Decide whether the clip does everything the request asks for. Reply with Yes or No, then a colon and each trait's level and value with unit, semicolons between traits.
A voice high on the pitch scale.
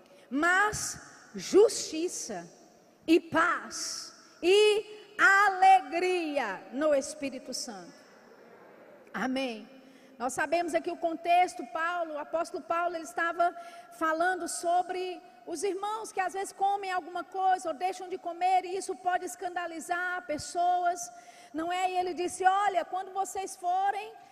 Yes: very high, 350 Hz